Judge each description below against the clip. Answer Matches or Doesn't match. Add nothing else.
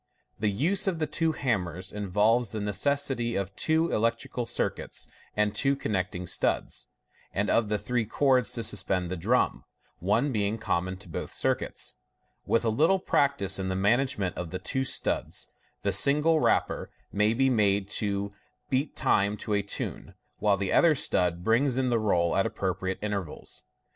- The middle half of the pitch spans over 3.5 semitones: Matches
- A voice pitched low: Matches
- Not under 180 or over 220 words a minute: Doesn't match